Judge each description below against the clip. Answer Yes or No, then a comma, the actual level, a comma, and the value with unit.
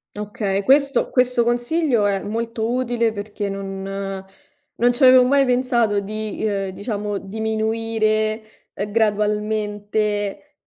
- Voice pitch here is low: No, high, 215 Hz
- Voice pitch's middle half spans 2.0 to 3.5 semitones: Yes, average, 2.7 semitones